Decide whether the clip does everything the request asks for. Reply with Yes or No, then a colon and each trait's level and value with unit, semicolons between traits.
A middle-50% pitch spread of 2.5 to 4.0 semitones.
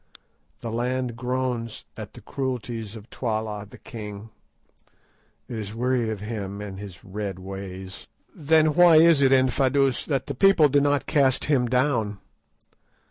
No: average, 4.6 semitones